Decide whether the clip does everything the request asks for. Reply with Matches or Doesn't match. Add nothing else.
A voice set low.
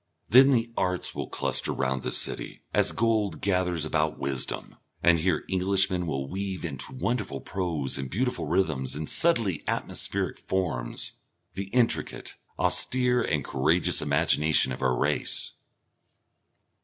Matches